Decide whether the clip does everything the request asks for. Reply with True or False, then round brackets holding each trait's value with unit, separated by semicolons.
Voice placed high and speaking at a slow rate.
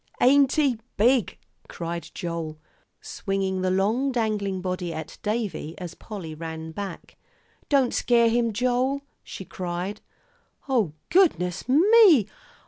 True (205 Hz; 120 wpm)